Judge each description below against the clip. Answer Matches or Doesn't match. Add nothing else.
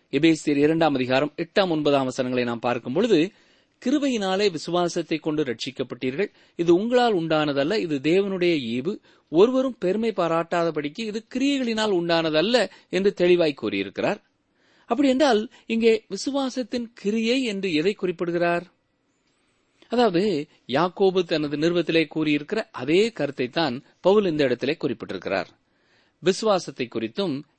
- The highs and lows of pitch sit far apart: Matches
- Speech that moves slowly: Doesn't match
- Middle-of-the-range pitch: Matches